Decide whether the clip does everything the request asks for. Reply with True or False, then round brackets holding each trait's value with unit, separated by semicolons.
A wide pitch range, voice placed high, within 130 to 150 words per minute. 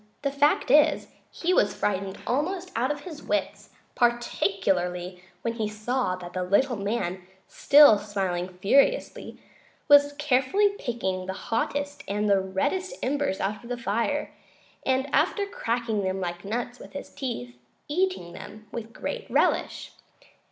True (6.9 semitones; 235 Hz; 140 wpm)